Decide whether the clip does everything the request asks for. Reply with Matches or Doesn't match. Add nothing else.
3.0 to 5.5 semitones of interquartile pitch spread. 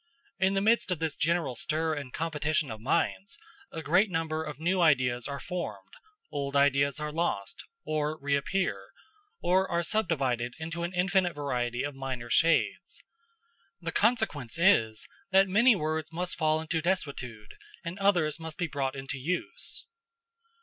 Matches